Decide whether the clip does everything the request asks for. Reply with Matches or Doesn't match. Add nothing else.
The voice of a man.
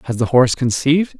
Matches